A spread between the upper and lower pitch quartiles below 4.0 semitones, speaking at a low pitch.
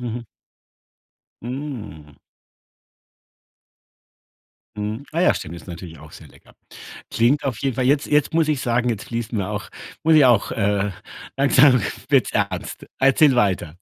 No: average, 5.3 semitones; low, 120 Hz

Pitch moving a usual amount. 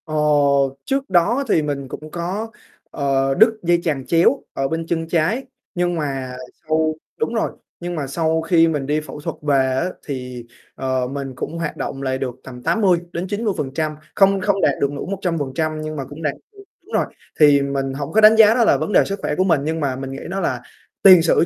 Yes: average, 4.8 semitones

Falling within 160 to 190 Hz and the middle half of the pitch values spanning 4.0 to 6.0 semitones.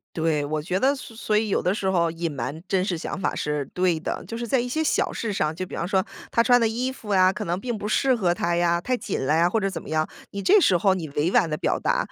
Yes: medium, 185 Hz; average, 5.2 semitones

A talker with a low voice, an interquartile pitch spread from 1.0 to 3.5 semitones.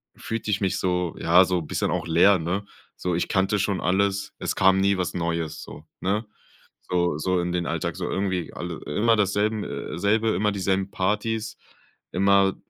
Yes: very low, 95 Hz; narrow, 2.4 semitones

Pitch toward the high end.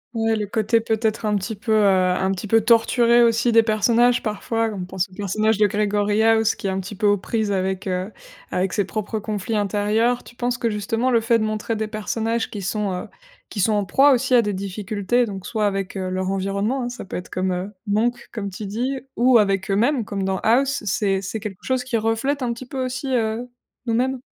Yes: high, 215 Hz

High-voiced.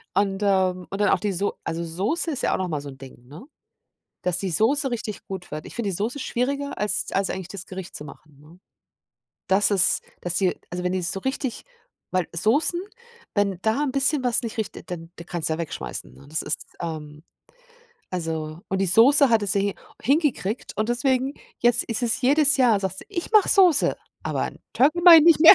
Yes: high, 200 Hz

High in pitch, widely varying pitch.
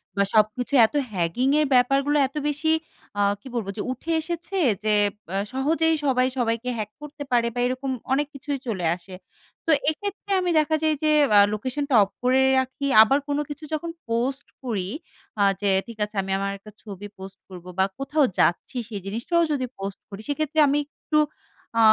Yes: very high, 255 Hz; wide, 5.7 semitones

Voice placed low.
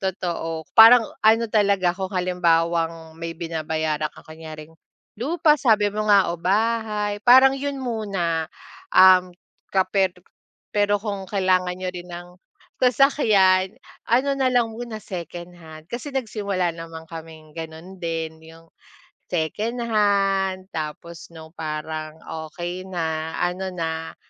No: medium, 185 Hz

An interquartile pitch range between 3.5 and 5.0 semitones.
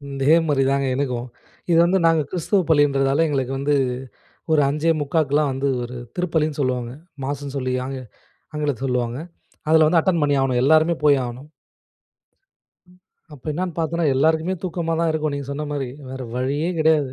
No: average, 3.0 semitones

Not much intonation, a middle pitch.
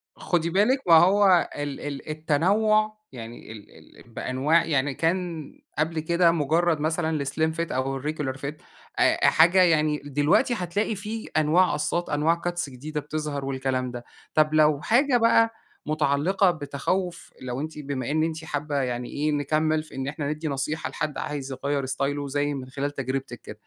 No: average, 3.2 semitones; medium, 150 Hz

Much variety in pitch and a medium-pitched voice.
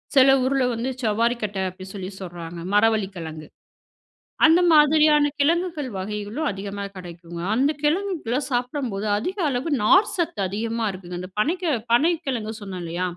No: wide, 7.7 semitones; high, 230 Hz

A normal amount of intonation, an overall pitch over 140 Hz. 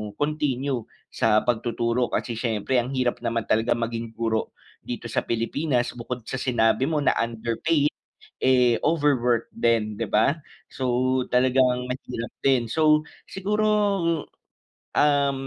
No: average, 3.3 semitones; low, 125 Hz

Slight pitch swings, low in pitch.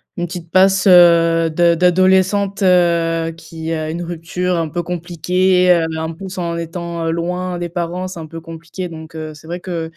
No: narrow, 1.6 semitones; medium, 170 Hz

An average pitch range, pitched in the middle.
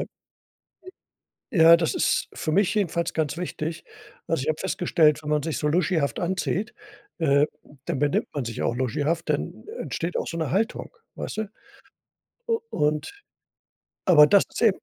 Yes: average, 3.2 semitones; medium, 165 Hz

